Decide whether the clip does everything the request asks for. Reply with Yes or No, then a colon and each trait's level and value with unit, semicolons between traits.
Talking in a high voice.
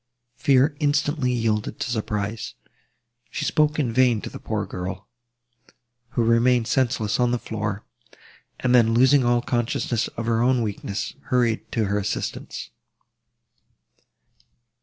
No: low, 120 Hz